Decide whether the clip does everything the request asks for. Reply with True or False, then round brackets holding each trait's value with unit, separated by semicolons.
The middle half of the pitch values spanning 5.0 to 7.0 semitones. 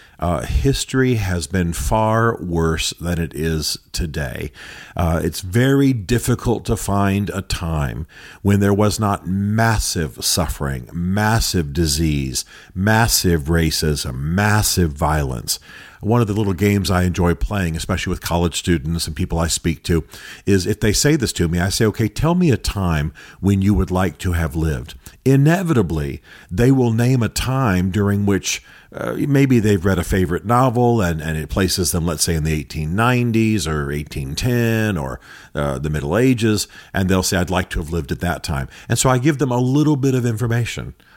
True (5.3 semitones)